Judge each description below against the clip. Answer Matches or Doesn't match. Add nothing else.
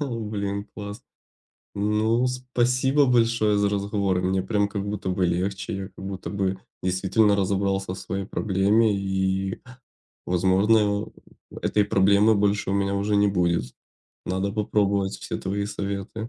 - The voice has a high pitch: Doesn't match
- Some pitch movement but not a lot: Doesn't match